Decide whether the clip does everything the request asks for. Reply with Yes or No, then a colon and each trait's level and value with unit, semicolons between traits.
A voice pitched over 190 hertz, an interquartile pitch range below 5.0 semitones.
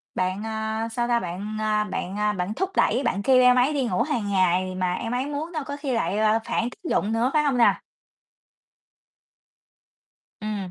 Yes: high, 220 Hz; average, 4.0 semitones